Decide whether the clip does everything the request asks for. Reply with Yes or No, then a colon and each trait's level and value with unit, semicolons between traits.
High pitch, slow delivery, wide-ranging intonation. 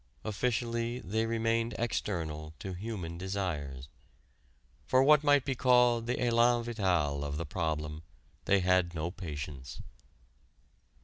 No: low, 100 Hz; slow, 120 wpm; wide, 6.9 semitones